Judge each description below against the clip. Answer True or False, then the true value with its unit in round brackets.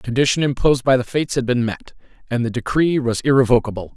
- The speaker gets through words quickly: True (210 wpm)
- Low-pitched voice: True (125 Hz)